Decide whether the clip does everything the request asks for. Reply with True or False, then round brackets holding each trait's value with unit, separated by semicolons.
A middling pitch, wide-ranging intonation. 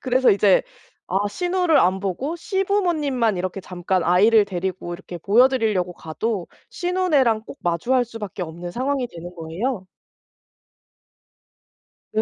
False (210 Hz; 6.6 semitones)